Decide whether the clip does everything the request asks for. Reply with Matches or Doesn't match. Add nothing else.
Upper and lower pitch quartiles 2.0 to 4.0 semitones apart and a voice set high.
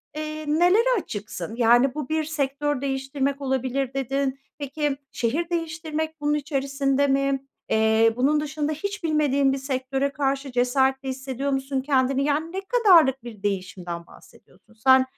Matches